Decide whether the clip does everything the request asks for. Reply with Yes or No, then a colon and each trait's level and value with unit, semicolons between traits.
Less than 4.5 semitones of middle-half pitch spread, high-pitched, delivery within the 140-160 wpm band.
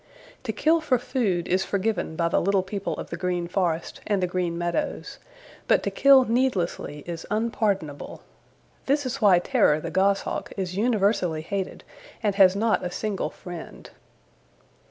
Yes: average, 4.1 semitones; high, 195 Hz; average, 155 wpm